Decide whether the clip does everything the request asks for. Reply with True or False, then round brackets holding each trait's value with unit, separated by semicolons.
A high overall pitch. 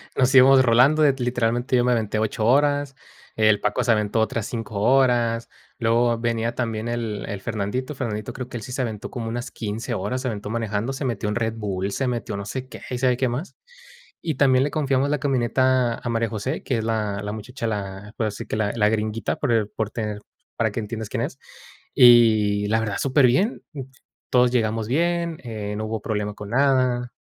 False (115 Hz)